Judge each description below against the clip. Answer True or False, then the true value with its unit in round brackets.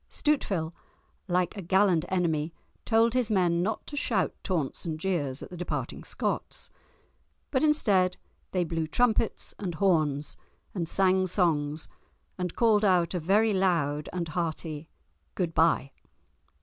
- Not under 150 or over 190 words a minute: False (135 wpm)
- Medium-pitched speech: True (180 Hz)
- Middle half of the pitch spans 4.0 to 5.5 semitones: False (3.5 semitones)